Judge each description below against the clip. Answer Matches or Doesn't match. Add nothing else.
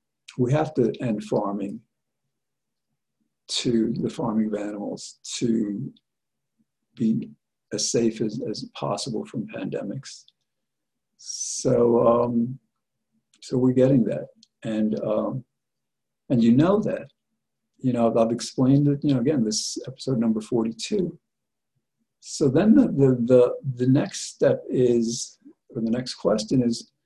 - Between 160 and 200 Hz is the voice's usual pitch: Doesn't match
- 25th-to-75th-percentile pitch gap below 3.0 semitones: Matches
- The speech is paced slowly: Matches